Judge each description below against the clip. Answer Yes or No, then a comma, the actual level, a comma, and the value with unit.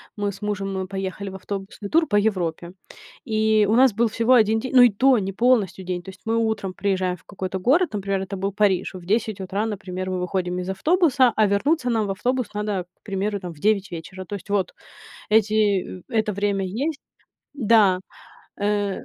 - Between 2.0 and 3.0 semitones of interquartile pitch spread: Yes, average, 2.7 semitones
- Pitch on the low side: No, high, 200 Hz